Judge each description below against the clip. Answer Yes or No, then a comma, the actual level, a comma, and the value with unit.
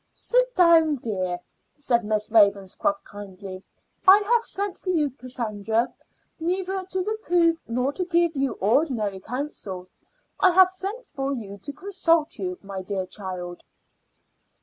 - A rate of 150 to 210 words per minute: No, slow, 135 wpm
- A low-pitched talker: No, very high, 270 Hz